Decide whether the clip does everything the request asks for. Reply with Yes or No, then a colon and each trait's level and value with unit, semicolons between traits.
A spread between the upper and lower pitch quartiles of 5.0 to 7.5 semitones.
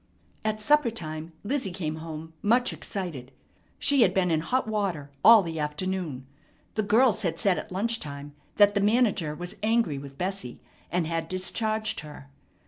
Yes: wide, 5.5 semitones